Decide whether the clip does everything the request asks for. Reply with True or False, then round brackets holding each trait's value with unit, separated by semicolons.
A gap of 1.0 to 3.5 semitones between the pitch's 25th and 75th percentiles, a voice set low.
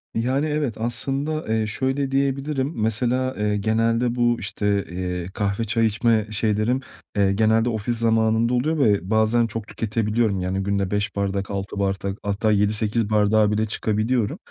True (2.8 semitones; 110 Hz)